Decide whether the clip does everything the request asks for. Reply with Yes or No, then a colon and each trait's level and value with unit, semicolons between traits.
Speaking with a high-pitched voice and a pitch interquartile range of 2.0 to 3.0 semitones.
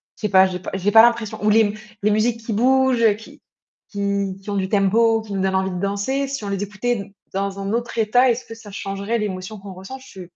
Yes: high, 205 Hz; narrow, 2.6 semitones